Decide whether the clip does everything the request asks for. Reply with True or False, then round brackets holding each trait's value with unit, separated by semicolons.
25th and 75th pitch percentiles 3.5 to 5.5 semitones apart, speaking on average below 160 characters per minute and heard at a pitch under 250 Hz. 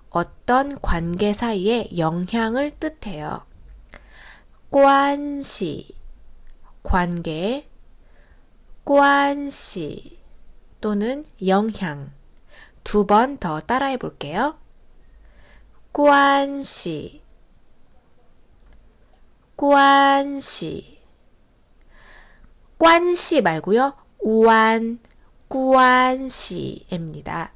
False (5.2 semitones; 105 characters per minute; 255 Hz)